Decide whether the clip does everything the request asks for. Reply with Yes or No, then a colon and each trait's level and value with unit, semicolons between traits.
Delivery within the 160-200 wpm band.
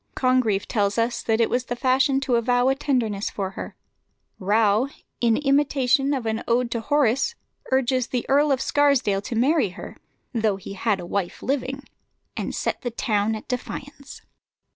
Yes: average, 175 wpm